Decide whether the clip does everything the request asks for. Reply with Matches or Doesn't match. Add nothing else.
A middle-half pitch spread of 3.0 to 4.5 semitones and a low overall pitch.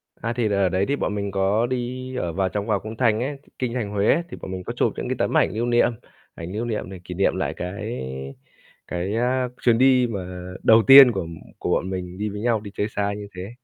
Matches